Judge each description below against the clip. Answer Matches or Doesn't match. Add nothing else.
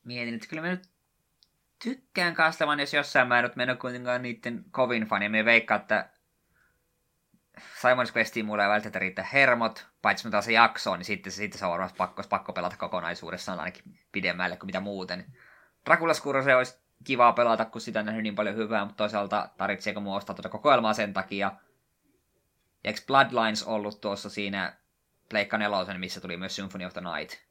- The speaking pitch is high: Doesn't match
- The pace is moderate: Doesn't match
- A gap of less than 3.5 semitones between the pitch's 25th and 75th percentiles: Doesn't match